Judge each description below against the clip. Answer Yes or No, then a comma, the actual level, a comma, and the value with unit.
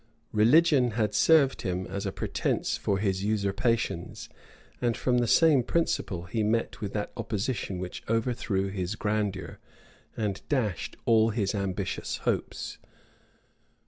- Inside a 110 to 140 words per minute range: Yes, slow, 135 wpm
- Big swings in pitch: No, average, 3.4 semitones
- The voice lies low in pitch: Yes, low, 105 Hz